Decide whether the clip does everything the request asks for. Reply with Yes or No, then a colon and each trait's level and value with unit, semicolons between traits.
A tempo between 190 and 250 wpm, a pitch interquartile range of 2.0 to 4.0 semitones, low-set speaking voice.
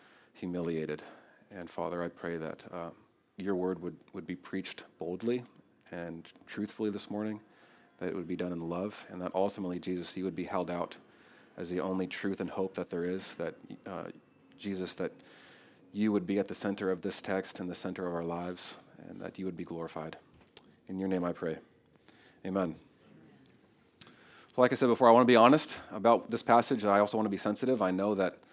Yes: fast, 205 wpm; average, 2.7 semitones; very low, 95 Hz